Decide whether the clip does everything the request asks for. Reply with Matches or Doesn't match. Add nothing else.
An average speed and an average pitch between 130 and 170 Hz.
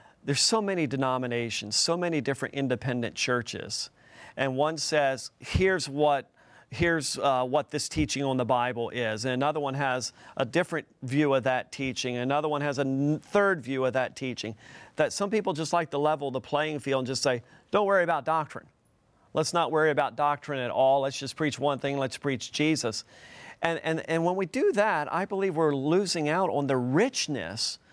Matches